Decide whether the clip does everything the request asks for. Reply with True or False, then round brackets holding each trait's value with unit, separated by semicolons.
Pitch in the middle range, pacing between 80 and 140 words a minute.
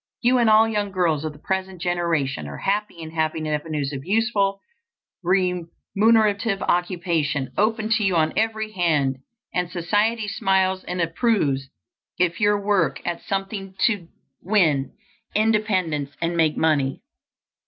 True (180 Hz; 135 wpm)